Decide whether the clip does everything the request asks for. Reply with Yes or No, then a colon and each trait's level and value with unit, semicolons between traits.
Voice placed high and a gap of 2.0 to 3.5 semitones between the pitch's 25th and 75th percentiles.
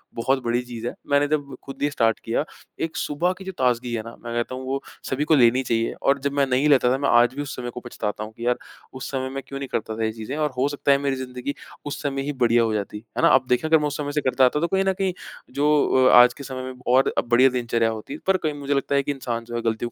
No: low, 130 Hz; average, 3.1 semitones